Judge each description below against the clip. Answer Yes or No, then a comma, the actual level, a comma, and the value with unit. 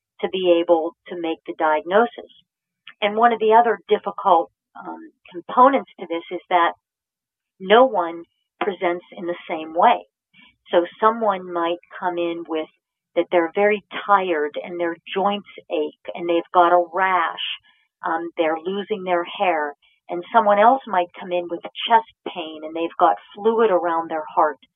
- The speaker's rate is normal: Yes, average, 160 wpm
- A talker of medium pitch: Yes, medium, 175 Hz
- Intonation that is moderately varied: Yes, average, 3.2 semitones